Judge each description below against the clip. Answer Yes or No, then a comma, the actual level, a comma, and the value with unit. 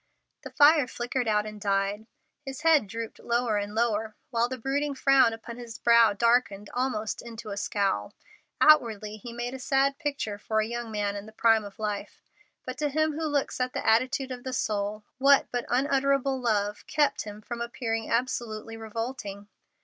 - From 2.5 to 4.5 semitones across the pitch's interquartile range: Yes, average, 3.7 semitones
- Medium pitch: No, high, 235 Hz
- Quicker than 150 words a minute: Yes, average, 180 wpm